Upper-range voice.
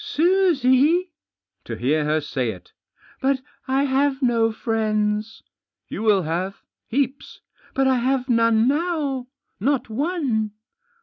Yes: very high, 250 Hz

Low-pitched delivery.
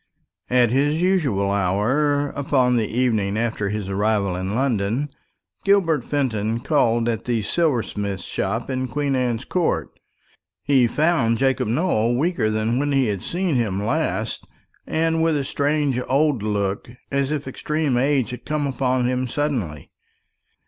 Yes: low, 125 Hz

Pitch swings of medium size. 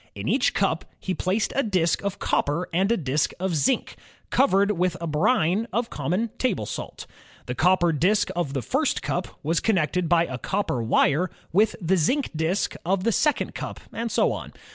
Yes: average, 4.6 semitones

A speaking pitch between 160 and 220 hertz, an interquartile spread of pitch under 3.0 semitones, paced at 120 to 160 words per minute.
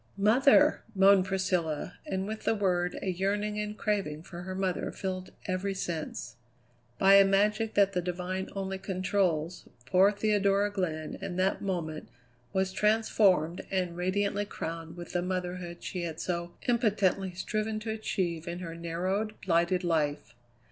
Yes: medium, 185 Hz; narrow, 2.6 semitones; average, 150 wpm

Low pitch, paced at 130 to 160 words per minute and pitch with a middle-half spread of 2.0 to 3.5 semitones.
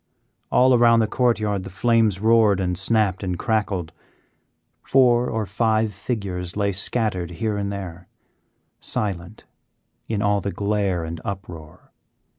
Yes: low, 100 Hz; slow, 135 wpm; average, 3.2 semitones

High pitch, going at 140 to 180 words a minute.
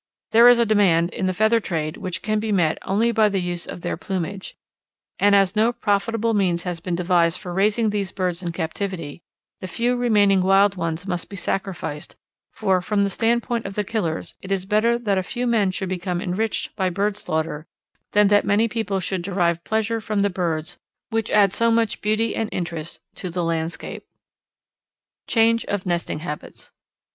No: high, 195 Hz; average, 190 wpm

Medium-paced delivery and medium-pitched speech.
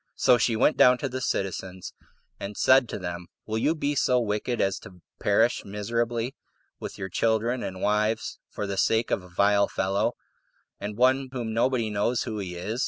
No: average, 185 wpm; low, 110 Hz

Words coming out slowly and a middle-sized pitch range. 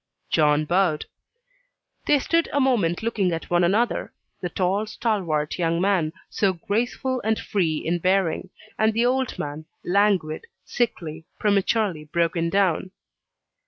Yes: slow, 130 wpm; average, 4.8 semitones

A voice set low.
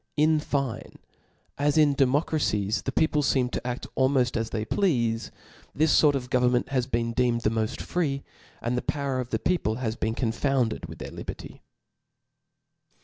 Yes: low, 125 Hz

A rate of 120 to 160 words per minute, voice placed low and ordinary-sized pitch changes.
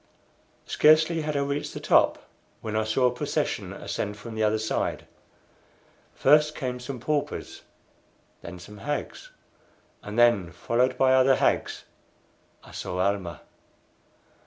Yes: slow, 135 wpm; low, 125 Hz; average, 5.0 semitones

